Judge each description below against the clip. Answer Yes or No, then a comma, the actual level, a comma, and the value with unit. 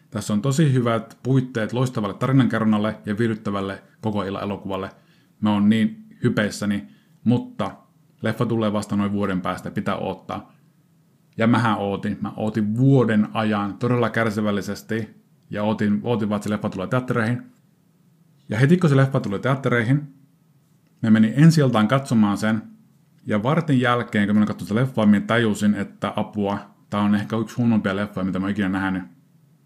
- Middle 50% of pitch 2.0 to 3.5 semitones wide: No, average, 4.6 semitones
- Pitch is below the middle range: Yes, low, 110 Hz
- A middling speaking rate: No, fast, 160 wpm